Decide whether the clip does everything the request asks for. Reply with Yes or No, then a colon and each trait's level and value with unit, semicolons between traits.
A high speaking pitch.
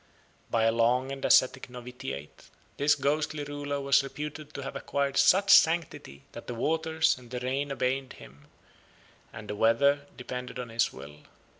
No: low, 135 Hz